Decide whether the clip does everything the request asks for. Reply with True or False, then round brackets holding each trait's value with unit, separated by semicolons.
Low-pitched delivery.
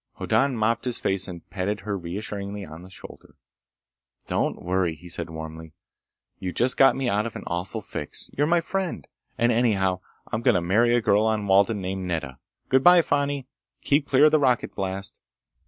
True (100 Hz)